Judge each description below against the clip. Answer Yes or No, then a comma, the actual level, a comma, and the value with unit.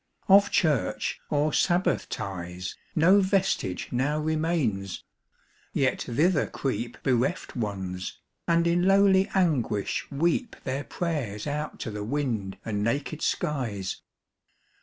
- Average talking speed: No, slow, 115 wpm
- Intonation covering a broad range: Yes, wide, 8.0 semitones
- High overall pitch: No, medium, 140 Hz